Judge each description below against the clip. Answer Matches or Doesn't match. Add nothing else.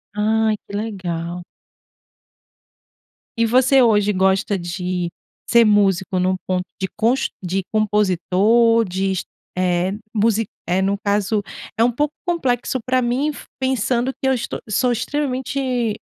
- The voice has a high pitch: Matches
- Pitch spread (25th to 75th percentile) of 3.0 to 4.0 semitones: Doesn't match